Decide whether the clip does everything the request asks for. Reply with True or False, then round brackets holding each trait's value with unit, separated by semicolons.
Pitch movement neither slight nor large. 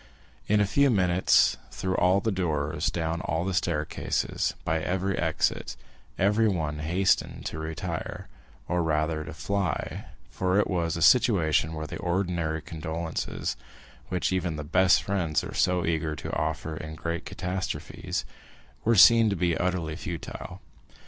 True (3.0 semitones)